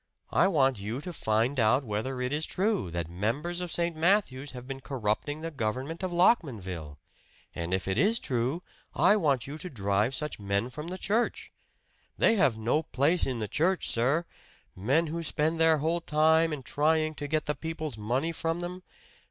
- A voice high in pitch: No, medium, 145 Hz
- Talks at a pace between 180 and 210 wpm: Yes, average, 185 wpm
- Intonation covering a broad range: Yes, wide, 6.1 semitones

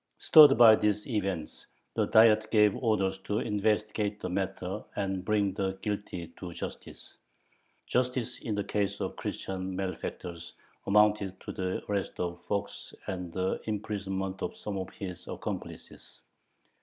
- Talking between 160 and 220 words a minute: No, average, 145 wpm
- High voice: No, low, 100 Hz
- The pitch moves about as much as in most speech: No, narrow, 2.1 semitones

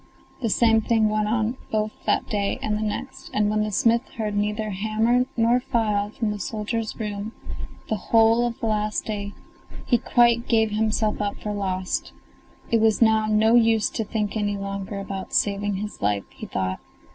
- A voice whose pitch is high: Yes, high, 215 Hz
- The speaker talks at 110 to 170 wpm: No, average, 180 wpm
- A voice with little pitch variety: Yes, narrow, 1.6 semitones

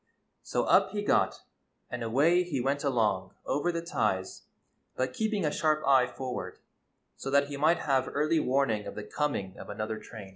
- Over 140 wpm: Yes, average, 180 wpm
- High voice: No, low, 135 Hz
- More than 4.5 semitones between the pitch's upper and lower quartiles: Yes, average, 5.3 semitones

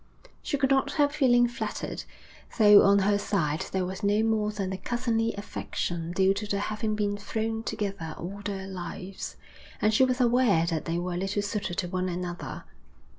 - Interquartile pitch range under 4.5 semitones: Yes, average, 3.2 semitones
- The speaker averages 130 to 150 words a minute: No, average, 180 wpm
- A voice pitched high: Yes, high, 205 Hz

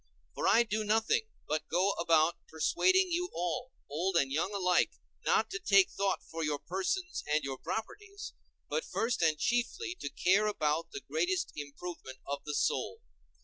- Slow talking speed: No, average, 165 wpm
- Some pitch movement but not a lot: No, wide, 8.3 semitones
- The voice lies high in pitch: Yes, high, 195 Hz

